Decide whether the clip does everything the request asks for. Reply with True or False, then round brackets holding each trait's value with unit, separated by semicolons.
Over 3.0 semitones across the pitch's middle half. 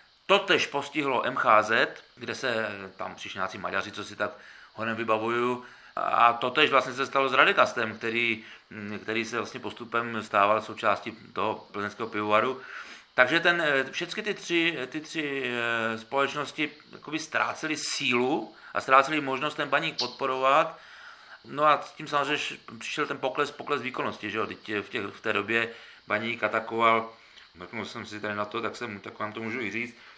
True (4.2 semitones)